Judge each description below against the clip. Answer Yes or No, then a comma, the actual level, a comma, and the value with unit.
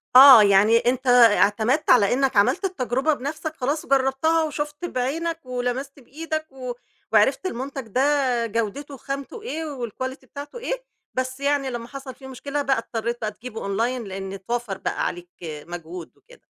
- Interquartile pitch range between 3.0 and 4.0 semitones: Yes, average, 3.7 semitones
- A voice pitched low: No, very high, 260 Hz